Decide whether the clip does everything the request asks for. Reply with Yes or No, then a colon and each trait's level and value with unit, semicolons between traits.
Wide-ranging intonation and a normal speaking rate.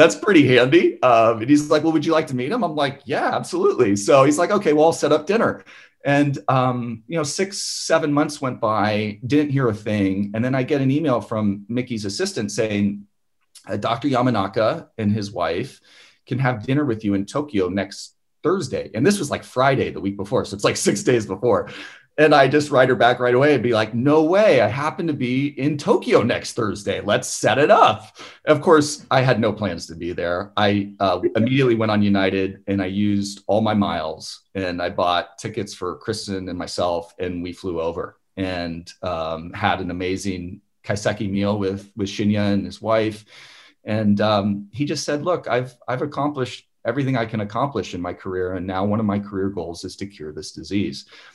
No: wide, 6.1 semitones; fast, 210 wpm